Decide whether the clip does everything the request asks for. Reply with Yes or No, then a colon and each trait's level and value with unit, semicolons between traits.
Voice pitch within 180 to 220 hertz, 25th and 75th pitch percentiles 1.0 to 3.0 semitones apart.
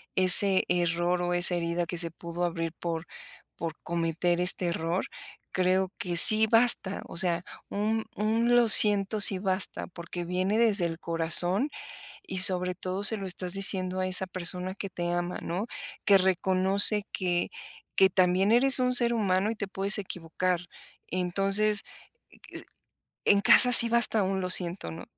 Yes: medium, 185 Hz; narrow, 2.6 semitones